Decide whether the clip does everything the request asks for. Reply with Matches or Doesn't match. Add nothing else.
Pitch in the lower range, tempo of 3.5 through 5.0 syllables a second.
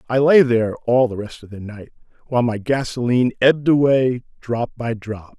Doesn't match